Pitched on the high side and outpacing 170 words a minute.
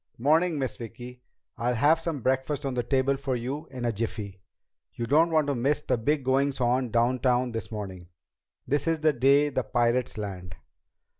No: low, 130 Hz; average, 180 wpm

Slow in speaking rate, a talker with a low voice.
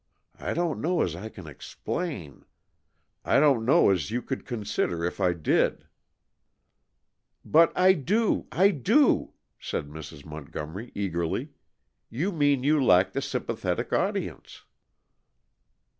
Yes: slow, 130 wpm; low, 120 Hz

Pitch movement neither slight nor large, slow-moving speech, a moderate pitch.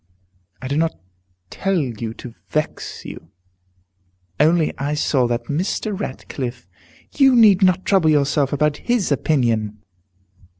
No: wide, 6.4 semitones; slow, 130 wpm; medium, 150 Hz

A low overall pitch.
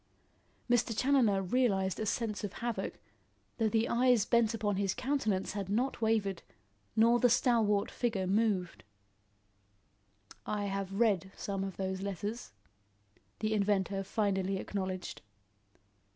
No: high, 205 Hz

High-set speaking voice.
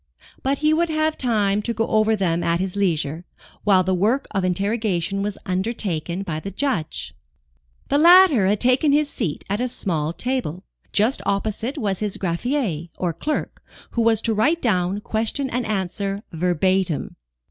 Yes: high, 205 Hz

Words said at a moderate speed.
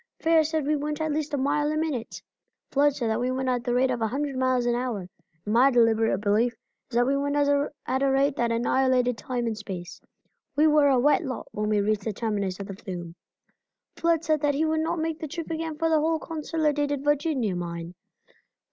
No: fast, 220 wpm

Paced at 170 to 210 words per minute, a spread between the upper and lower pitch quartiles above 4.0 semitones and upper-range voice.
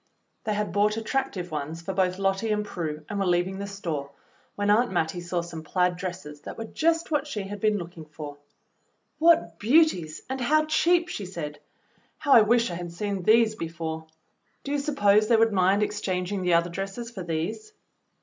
Yes: average, 190 wpm; average, 4.6 semitones; high, 195 Hz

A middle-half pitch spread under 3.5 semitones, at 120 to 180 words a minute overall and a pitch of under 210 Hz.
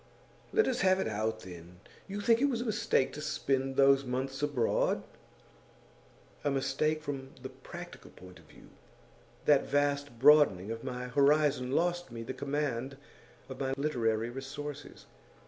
Yes: average, 3.0 semitones; average, 150 wpm; low, 135 Hz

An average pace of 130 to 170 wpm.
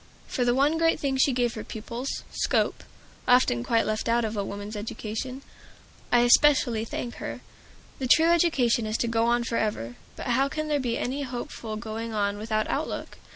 No: average, 180 wpm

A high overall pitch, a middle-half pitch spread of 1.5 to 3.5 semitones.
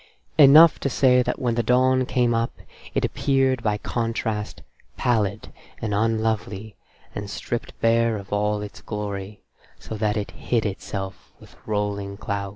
No: low, 110 Hz; average, 2.7 semitones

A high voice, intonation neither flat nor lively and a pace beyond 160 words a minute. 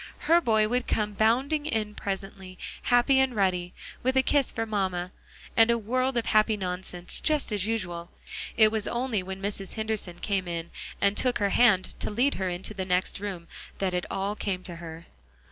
Yes: high, 205 Hz; average, 4.1 semitones; average, 190 wpm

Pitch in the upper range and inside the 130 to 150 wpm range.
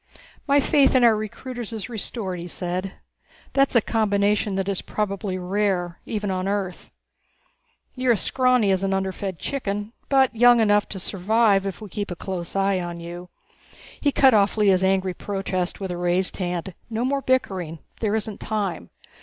No: high, 200 Hz; average, 170 wpm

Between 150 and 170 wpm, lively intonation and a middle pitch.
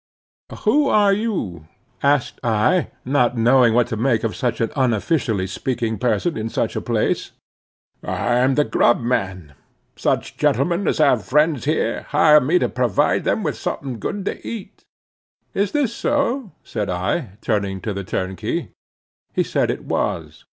No: average, 160 wpm; wide, 7.0 semitones; low, 125 Hz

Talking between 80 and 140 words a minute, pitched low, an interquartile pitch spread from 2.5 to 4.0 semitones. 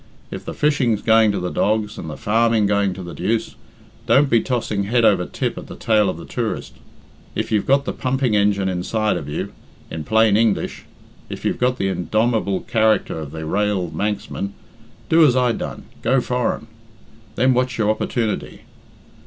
No: average, 180 wpm; low, 110 Hz; average, 3.3 semitones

